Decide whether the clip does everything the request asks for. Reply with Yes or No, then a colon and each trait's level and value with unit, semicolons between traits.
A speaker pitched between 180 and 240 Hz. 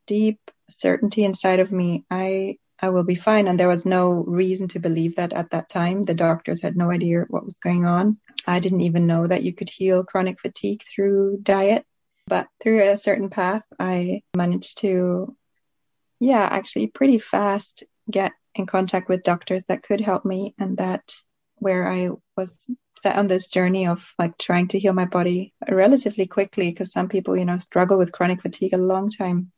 Yes: medium, 185 Hz